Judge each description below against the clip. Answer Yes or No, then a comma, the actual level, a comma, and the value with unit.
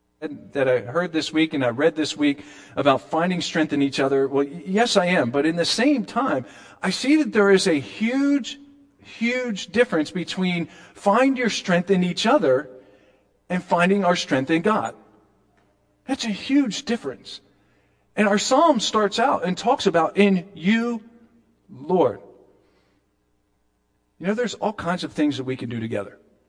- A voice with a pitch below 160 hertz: No, medium, 175 Hz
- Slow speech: No, average, 170 wpm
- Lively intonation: Yes, wide, 8.3 semitones